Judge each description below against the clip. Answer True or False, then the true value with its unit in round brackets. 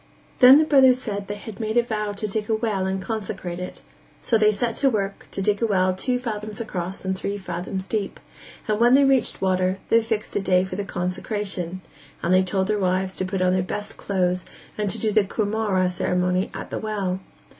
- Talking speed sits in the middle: False (220 wpm)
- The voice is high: True (200 Hz)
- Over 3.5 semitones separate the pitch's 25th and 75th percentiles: False (2.7 semitones)